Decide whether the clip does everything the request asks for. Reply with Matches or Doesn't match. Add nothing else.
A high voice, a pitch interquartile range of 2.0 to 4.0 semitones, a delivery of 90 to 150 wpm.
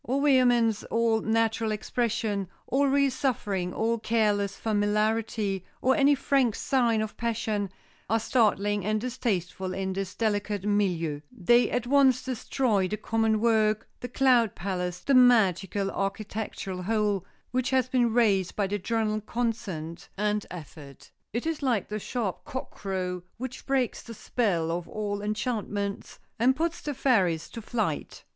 Matches